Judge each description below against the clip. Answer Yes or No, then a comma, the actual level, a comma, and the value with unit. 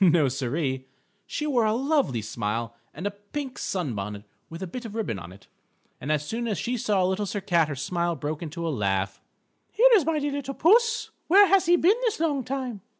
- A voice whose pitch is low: No, high, 195 Hz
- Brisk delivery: Yes, fast, 215 wpm